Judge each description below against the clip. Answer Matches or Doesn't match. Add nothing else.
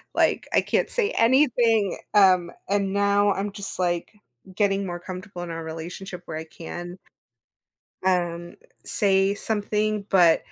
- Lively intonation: Doesn't match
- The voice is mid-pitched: Doesn't match